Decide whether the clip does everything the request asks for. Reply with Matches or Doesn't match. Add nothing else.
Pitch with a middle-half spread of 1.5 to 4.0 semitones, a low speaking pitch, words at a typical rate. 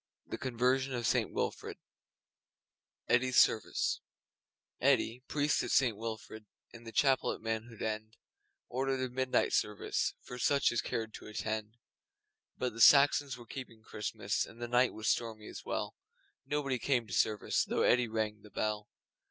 Matches